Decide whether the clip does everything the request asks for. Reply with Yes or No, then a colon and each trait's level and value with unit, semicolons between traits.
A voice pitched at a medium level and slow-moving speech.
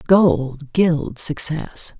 Yes: medium, 155 Hz; slow, 90 wpm